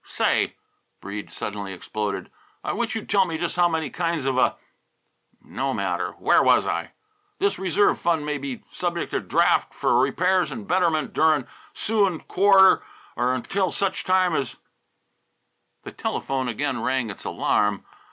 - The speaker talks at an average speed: Yes, average, 155 wpm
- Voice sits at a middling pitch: Yes, medium, 160 Hz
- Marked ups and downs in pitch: Yes, wide, 6.4 semitones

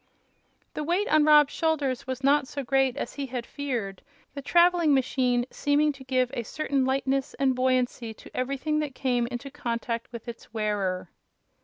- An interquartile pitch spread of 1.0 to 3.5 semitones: Yes, average, 2.9 semitones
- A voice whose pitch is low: No, very high, 265 Hz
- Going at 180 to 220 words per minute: No, average, 170 wpm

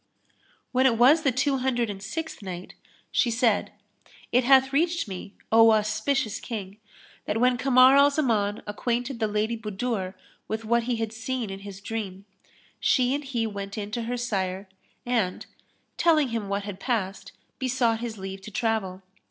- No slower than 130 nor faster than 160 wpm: No, average, 170 wpm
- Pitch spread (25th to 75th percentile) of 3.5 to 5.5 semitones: Yes, average, 3.8 semitones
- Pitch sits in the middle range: No, high, 225 Hz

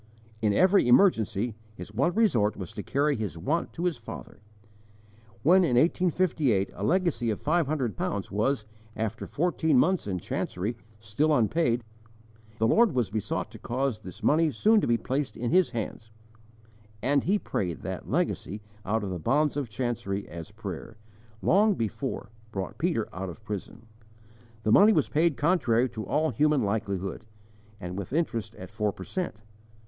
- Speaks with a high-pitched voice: No, low, 120 Hz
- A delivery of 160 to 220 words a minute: Yes, average, 165 wpm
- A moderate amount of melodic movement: No, wide, 7.0 semitones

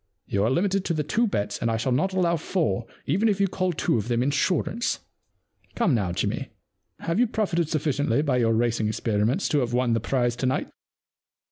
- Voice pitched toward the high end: No, medium, 140 Hz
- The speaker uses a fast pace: Yes, fast, 210 wpm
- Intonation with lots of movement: Yes, wide, 7.7 semitones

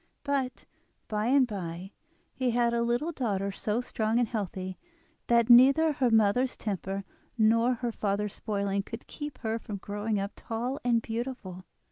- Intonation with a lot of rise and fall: No, average, 3.5 semitones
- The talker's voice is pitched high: Yes, high, 225 Hz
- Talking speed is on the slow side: No, average, 155 wpm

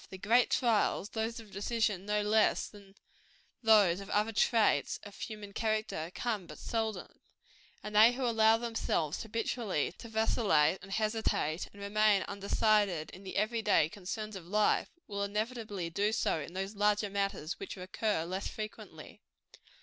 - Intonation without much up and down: Yes, narrow, 2.2 semitones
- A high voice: Yes, high, 210 Hz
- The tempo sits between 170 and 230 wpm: No, average, 155 wpm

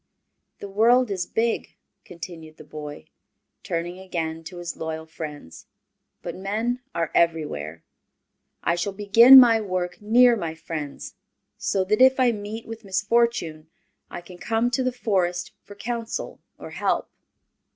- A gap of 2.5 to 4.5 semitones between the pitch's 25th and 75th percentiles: No, wide, 5.6 semitones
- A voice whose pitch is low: No, high, 190 Hz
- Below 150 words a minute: Yes, average, 140 wpm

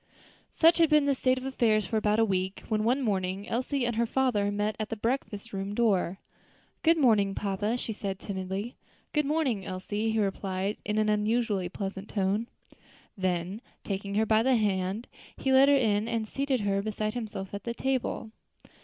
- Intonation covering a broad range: No, average, 3.4 semitones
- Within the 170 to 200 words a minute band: Yes, average, 190 wpm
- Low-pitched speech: No, high, 215 Hz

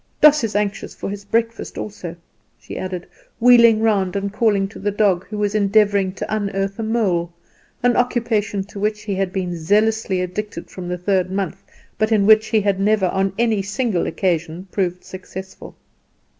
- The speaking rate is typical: Yes, average, 175 wpm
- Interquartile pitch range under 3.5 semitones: Yes, narrow, 2.4 semitones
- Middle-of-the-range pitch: No, high, 200 Hz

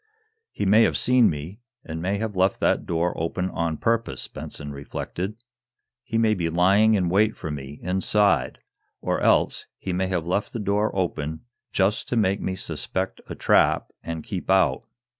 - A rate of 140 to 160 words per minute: No, average, 175 wpm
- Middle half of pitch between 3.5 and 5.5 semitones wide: Yes, average, 4.1 semitones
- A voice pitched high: No, very low, 95 Hz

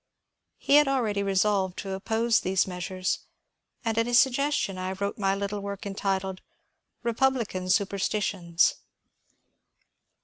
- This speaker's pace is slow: Yes, slow, 125 wpm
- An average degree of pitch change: Yes, average, 3.2 semitones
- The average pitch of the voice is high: Yes, high, 200 Hz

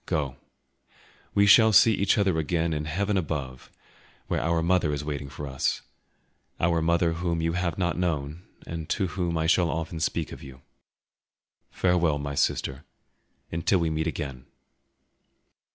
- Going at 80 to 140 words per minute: No, average, 150 wpm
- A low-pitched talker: Yes, very low, 80 Hz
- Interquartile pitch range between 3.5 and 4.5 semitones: No, average, 3.1 semitones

